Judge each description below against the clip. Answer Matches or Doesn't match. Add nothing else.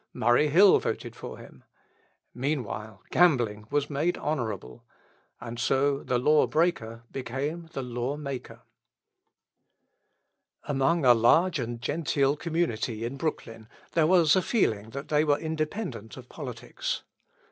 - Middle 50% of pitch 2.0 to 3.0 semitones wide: Doesn't match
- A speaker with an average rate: Doesn't match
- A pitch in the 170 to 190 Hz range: Doesn't match